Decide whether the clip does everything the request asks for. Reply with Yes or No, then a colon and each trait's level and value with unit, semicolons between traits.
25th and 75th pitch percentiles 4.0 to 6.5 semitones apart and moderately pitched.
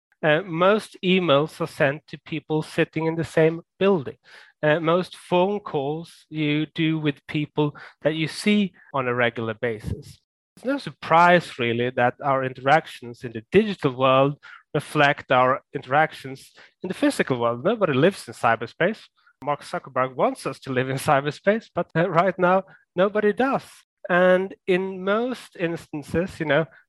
Yes: average, 4.8 semitones; medium, 160 Hz